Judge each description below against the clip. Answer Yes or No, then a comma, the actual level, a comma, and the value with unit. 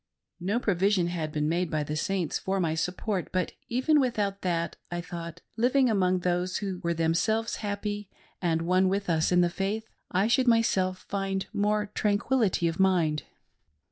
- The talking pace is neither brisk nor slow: Yes, average, 170 wpm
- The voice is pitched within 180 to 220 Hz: Yes, medium, 185 Hz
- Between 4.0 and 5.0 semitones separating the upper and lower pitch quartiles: No, average, 3.2 semitones